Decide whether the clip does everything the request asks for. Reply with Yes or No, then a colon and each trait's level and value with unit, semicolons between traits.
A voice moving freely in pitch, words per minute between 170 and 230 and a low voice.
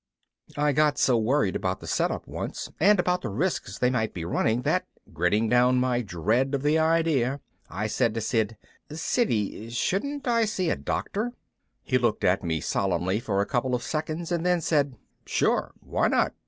Yes: wide, 6.8 semitones; average, 185 wpm; low, 125 Hz